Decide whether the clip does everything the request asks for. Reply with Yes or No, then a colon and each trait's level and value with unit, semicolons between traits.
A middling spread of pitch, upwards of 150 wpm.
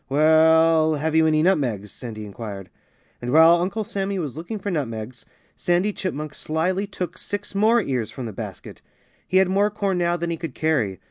No: wide, 5.7 semitones; average, 185 wpm